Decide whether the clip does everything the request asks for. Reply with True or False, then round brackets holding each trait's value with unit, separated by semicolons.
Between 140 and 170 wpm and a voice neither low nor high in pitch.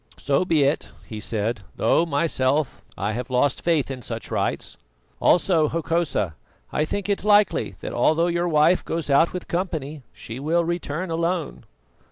True (160 wpm; 155 Hz)